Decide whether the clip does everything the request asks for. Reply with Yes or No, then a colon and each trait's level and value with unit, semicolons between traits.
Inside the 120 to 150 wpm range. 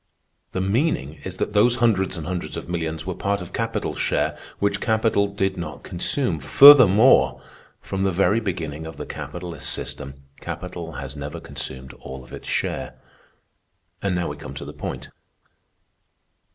No: average, 160 wpm